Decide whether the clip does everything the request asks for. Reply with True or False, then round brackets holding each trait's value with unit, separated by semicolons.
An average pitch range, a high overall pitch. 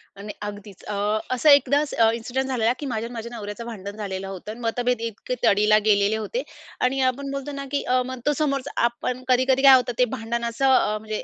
True (3.6 semitones; 235 Hz)